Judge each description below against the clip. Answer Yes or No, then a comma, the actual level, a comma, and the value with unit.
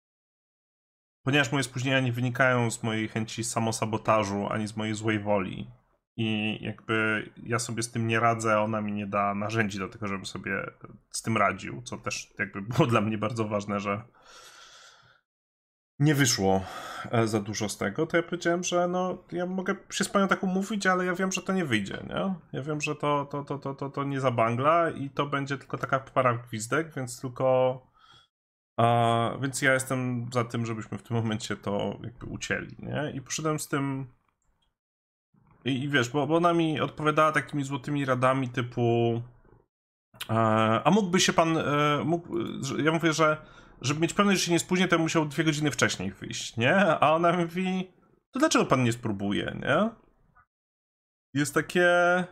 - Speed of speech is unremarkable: No, fast, 175 wpm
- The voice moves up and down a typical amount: No, wide, 6.4 semitones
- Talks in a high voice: No, low, 135 Hz